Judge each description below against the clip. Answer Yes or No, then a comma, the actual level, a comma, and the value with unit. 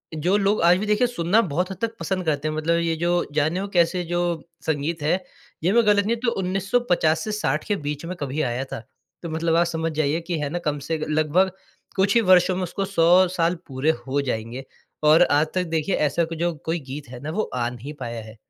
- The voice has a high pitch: No, medium, 165 Hz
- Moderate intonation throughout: Yes, average, 3.7 semitones